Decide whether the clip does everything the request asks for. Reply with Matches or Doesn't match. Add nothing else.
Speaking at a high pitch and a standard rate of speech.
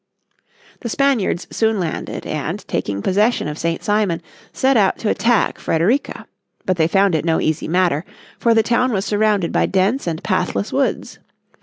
Matches